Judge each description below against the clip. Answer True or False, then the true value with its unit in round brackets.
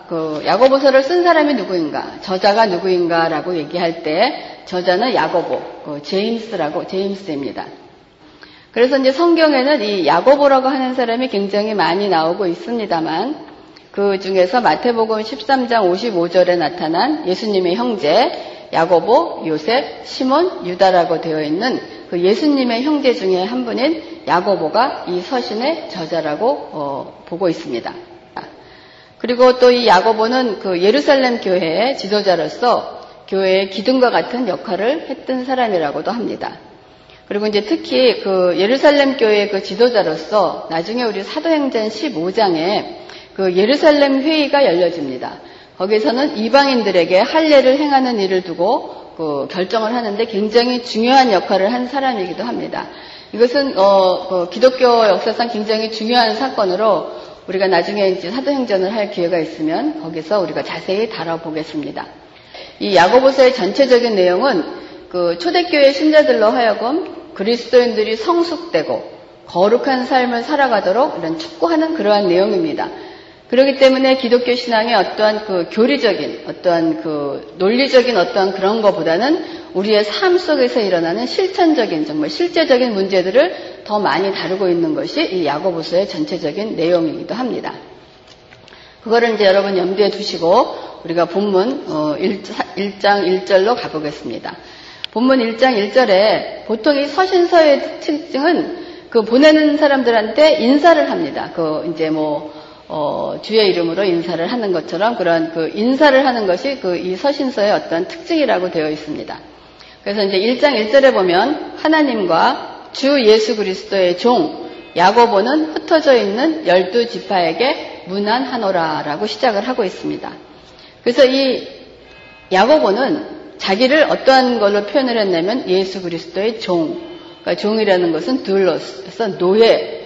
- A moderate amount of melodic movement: False (6.9 semitones)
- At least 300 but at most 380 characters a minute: True (320 characters per minute)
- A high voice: True (225 Hz)